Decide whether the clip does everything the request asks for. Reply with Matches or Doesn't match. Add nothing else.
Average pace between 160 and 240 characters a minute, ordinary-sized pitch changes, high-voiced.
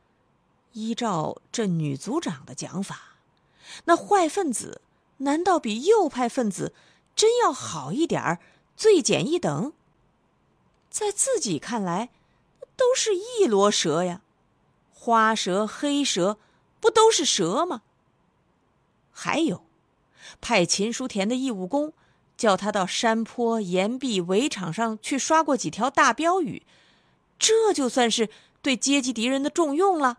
Doesn't match